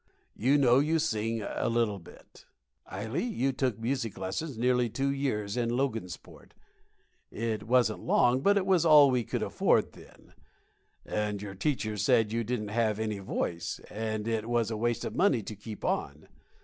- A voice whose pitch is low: Yes, low, 115 Hz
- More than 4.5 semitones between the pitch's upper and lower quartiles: No, average, 3.7 semitones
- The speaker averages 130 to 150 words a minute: No, average, 170 wpm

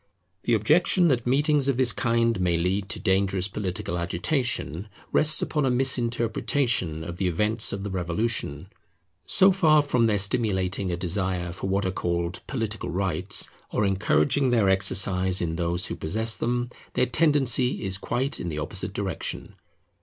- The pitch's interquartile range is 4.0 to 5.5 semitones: Yes, average, 5.2 semitones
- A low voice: Yes, low, 100 Hz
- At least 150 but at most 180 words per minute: Yes, average, 160 wpm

